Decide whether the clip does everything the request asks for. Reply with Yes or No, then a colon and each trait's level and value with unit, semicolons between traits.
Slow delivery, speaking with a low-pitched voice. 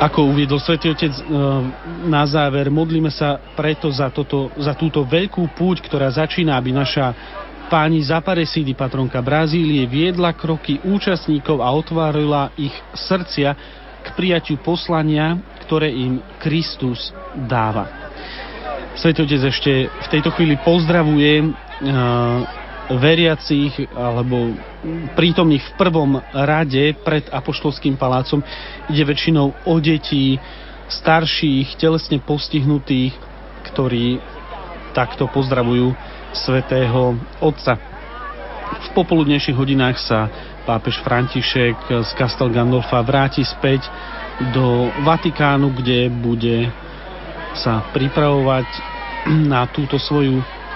No: slow, 100 wpm; medium, 145 Hz